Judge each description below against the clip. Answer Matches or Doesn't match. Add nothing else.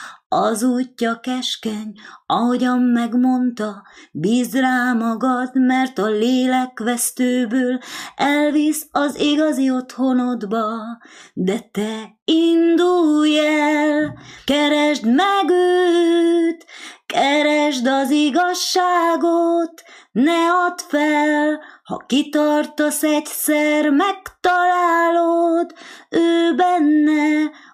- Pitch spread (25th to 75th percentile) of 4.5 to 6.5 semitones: Matches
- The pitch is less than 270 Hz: Doesn't match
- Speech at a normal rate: Doesn't match